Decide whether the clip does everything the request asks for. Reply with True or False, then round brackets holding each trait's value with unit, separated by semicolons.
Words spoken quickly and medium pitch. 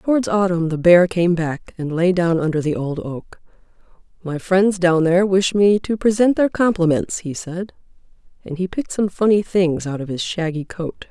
False (195 wpm; 180 Hz)